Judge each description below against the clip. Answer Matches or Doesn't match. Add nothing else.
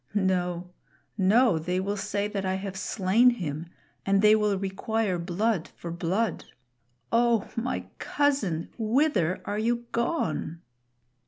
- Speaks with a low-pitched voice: Doesn't match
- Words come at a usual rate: Doesn't match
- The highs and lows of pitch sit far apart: Doesn't match